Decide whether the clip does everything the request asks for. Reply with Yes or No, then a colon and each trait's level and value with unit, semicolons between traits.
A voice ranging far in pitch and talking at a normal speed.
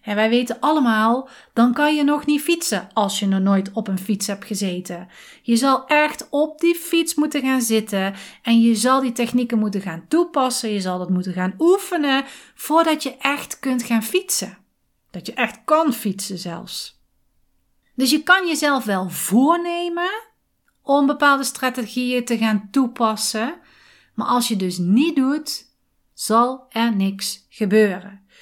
Yes: wide, 5.9 semitones; average, 160 wpm